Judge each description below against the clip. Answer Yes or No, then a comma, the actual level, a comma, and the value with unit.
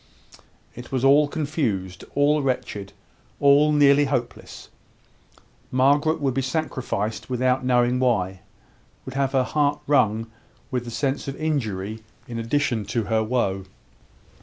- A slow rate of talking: Yes, slow, 130 wpm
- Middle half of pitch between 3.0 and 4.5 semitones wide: Yes, average, 4.1 semitones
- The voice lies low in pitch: Yes, low, 130 Hz